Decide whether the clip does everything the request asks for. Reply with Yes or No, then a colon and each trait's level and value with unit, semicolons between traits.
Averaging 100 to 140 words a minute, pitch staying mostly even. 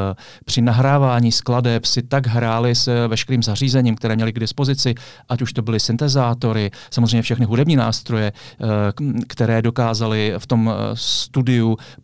Yes: average, 135 wpm; narrow, 2.0 semitones